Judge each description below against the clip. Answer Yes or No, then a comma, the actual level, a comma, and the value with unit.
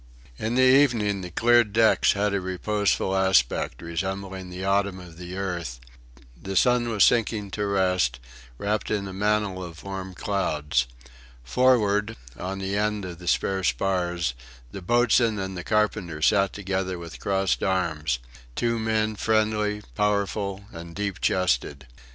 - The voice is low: Yes, very low, 95 Hz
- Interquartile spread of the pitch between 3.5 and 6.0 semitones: No, average, 2.8 semitones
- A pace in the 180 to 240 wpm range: No, average, 145 wpm